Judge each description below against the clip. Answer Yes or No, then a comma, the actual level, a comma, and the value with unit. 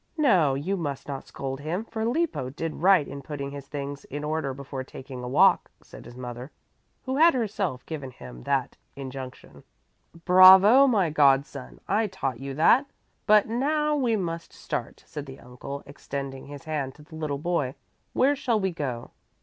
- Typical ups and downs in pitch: No, wide, 6.5 semitones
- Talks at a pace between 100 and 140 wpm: No, average, 175 wpm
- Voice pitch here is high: No, medium, 150 Hz